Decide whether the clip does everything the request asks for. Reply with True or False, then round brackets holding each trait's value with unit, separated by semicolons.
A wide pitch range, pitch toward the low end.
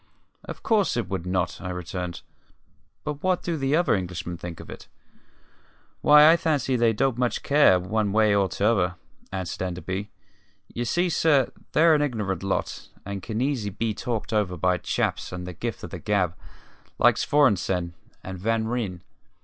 True (6.7 semitones; 105 Hz)